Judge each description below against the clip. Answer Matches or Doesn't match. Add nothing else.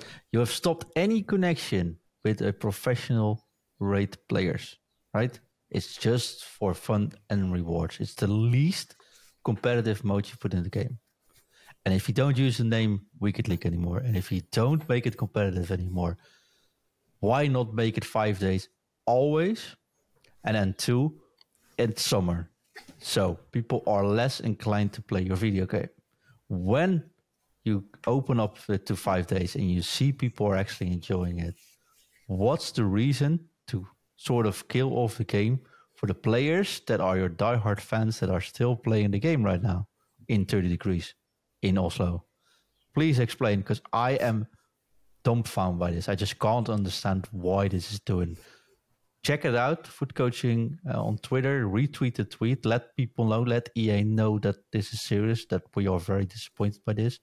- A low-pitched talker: Matches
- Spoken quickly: Doesn't match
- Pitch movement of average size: Matches